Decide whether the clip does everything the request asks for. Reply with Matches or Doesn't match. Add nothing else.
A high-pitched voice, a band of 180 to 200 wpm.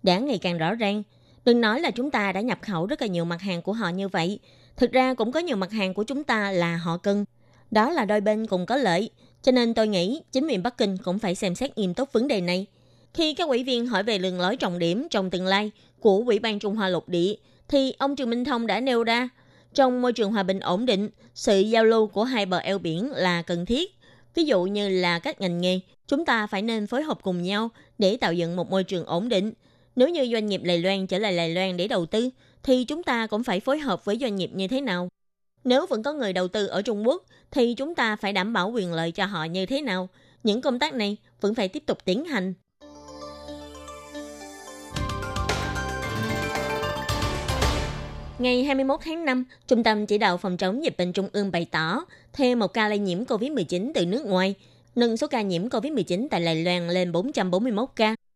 Doesn't match